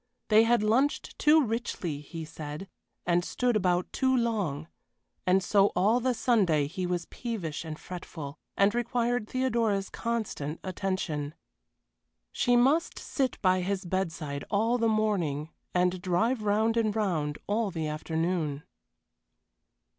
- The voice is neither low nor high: No, high, 195 Hz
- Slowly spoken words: Yes, slow, 130 wpm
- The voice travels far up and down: Yes, wide, 5.8 semitones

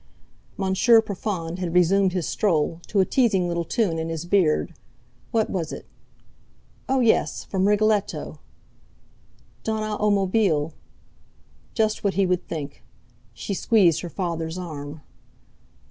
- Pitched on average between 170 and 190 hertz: Yes, medium, 185 Hz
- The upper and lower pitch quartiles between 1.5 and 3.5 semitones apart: No, average, 4.1 semitones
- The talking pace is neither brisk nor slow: No, slow, 130 wpm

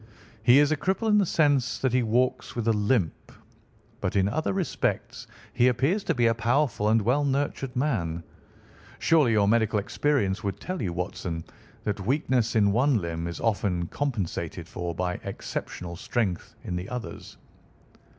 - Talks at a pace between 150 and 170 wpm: Yes, average, 165 wpm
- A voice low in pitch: Yes, low, 115 Hz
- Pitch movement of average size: No, wide, 6.0 semitones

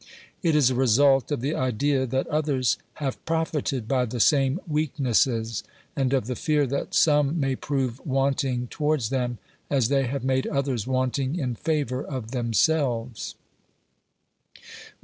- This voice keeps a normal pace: Yes, average, 145 wpm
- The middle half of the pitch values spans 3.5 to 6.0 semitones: No, narrow, 2.6 semitones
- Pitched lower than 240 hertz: Yes, low, 135 Hz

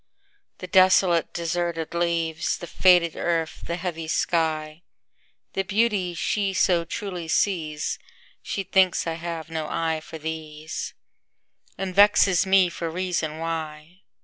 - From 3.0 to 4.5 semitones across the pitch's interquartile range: No, narrow, 2.4 semitones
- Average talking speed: No, slow, 110 wpm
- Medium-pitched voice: Yes, medium, 170 Hz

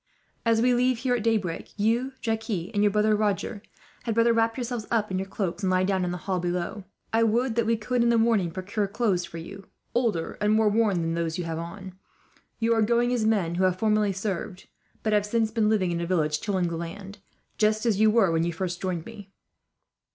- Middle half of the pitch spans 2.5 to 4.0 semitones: Yes, average, 3.7 semitones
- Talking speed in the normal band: No, fast, 230 wpm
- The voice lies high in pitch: Yes, high, 210 Hz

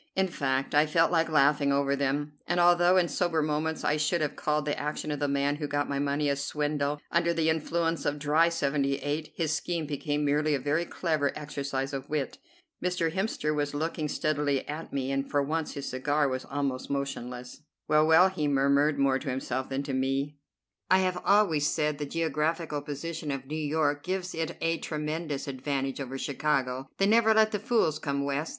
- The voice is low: No, medium, 150 Hz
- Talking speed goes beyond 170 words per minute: Yes, average, 195 wpm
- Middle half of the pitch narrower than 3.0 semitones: Yes, narrow, 2.5 semitones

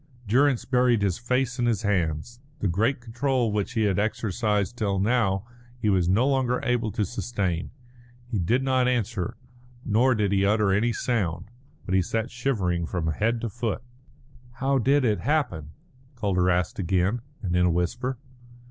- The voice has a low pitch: Yes, low, 110 Hz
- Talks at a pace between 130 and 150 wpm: No, average, 165 wpm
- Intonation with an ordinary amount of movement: Yes, average, 4.4 semitones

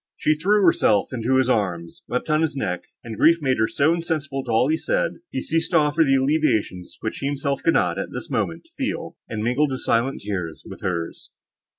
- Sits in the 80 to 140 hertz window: Yes, low, 135 Hz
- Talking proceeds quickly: Yes, fast, 220 wpm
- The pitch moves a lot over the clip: Yes, wide, 5.9 semitones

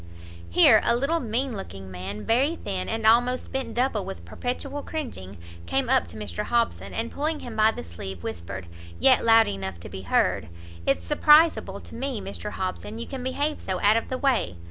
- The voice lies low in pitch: No, high, 225 Hz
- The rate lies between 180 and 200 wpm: Yes, average, 190 wpm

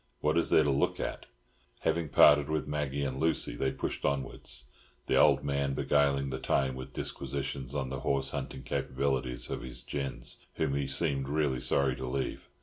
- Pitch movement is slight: Yes, narrow, 1.4 semitones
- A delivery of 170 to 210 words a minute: Yes, average, 180 wpm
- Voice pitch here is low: Yes, very low, 70 Hz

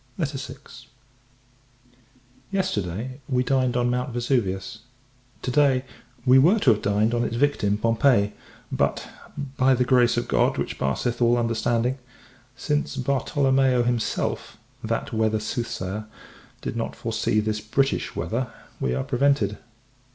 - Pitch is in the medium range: No, low, 120 Hz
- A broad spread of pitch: No, average, 3.3 semitones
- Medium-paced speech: No, slow, 130 wpm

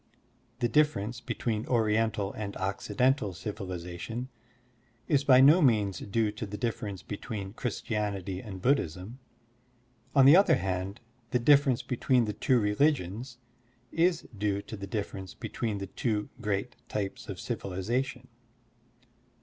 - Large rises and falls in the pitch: No, average, 4.4 semitones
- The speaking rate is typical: No, slow, 125 wpm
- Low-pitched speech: Yes, low, 110 Hz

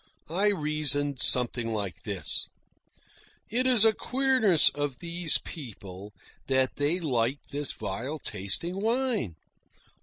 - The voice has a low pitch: No, medium, 145 Hz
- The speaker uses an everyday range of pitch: No, wide, 8.2 semitones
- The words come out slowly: Yes, slow, 115 wpm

